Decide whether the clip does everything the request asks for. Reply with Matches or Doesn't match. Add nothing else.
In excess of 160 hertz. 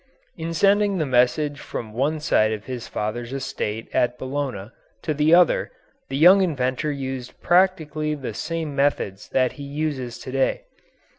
Doesn't match